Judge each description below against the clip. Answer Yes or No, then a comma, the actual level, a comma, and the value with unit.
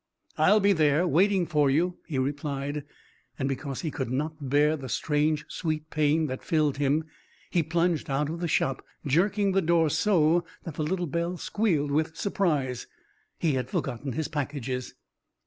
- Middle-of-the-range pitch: Yes, medium, 155 Hz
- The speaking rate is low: No, average, 165 wpm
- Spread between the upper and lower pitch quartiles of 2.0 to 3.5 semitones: Yes, average, 3.2 semitones